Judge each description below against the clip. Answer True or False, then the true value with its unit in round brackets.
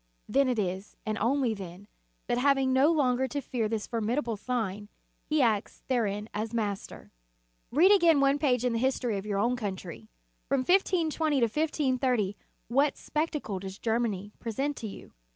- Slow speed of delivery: False (165 wpm)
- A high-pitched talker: True (240 Hz)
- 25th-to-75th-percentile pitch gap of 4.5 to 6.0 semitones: True (4.9 semitones)